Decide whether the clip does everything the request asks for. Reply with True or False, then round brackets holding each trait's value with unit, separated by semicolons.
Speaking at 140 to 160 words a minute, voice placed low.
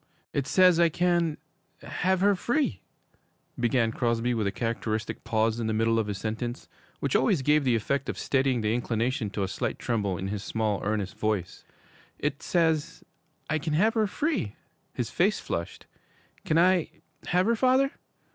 False (170 wpm; 125 Hz)